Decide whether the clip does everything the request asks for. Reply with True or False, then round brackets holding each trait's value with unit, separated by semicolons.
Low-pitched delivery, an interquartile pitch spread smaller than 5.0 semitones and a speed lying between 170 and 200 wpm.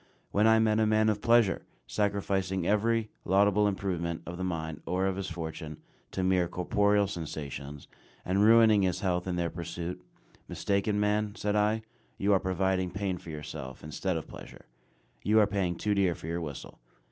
True (95 Hz; 3.2 semitones; 175 wpm)